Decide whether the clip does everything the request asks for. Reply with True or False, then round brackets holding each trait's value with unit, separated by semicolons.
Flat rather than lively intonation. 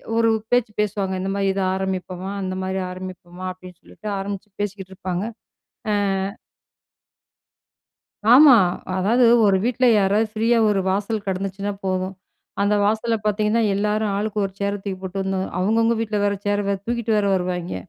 True (2.3 semitones)